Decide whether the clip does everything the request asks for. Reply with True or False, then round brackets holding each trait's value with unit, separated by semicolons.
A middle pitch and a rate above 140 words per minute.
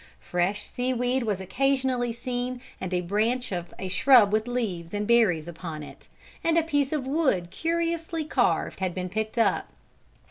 False (235 Hz; 165 wpm)